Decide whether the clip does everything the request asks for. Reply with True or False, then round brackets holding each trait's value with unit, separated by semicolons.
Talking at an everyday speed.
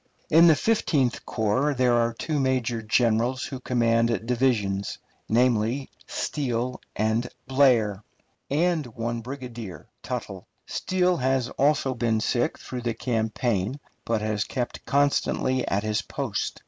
False (125 wpm)